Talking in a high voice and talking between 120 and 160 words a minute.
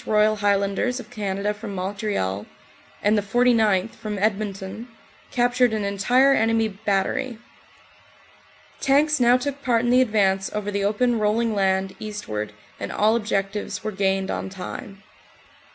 Yes: high, 210 Hz; average, 145 wpm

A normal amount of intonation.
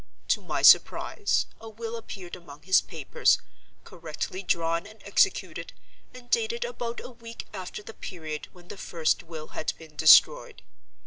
No: wide, 6.0 semitones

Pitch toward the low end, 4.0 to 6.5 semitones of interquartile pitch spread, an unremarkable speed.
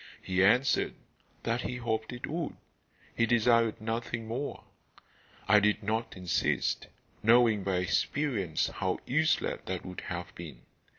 No: low, 110 Hz; average, 4.3 semitones; slow, 130 wpm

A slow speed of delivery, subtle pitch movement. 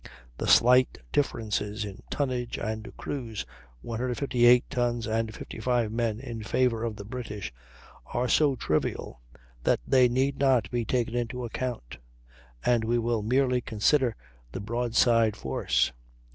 Yes: slow, 130 wpm; narrow, 2.3 semitones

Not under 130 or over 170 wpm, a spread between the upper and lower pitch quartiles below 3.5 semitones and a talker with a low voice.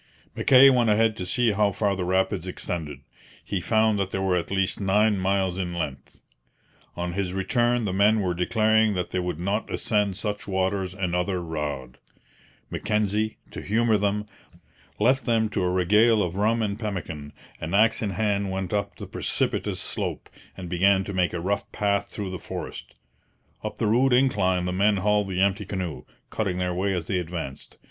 No: average, 185 wpm; average, 2.8 semitones; low, 100 Hz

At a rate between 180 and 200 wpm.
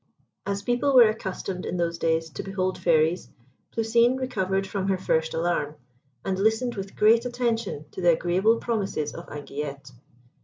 No: average, 155 wpm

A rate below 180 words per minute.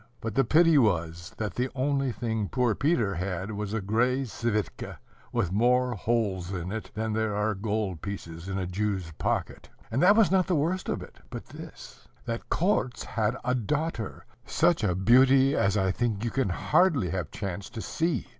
No: average, 185 wpm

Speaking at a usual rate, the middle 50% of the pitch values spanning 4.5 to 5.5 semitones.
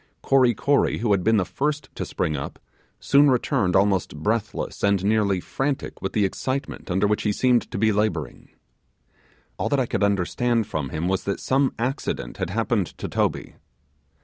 Yes: average, 175 wpm; average, 4.9 semitones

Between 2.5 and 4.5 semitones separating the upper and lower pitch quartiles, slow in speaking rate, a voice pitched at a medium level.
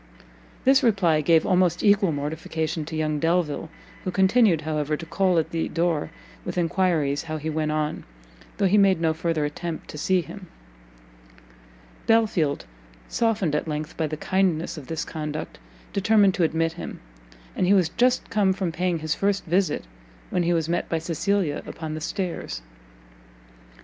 No: average, 3.3 semitones; average, 165 wpm; medium, 165 Hz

